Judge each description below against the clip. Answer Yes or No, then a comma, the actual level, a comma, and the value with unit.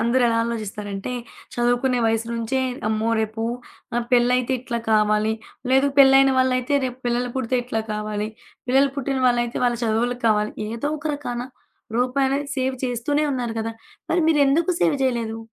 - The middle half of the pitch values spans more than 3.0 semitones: No, average, 2.7 semitones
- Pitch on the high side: Yes, high, 245 Hz